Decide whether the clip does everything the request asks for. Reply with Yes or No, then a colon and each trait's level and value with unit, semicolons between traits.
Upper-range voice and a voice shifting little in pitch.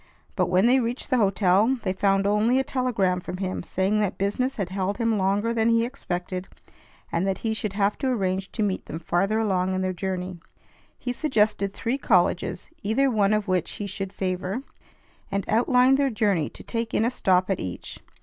No: high, 200 Hz; average, 3.6 semitones